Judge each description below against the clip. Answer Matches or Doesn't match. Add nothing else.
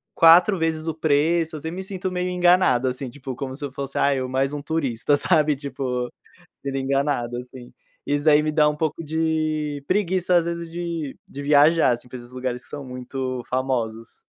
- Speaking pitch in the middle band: Matches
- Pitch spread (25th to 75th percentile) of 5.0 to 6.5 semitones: Doesn't match